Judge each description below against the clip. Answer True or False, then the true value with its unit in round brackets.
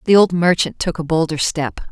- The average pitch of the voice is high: False (165 Hz)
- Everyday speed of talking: False (220 wpm)